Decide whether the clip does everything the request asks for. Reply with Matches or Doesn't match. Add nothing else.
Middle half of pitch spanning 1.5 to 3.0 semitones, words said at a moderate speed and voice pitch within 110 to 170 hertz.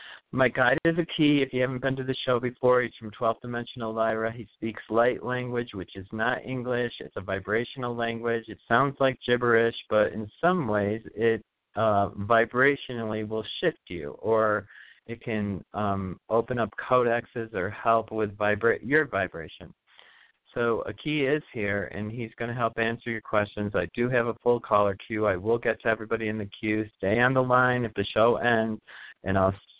Matches